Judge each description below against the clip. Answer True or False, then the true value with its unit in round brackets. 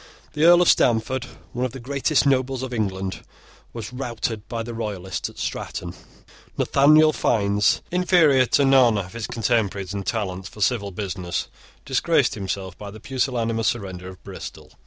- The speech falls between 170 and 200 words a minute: False (155 wpm)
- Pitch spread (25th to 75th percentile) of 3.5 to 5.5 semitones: True (4.7 semitones)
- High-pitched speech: False (115 Hz)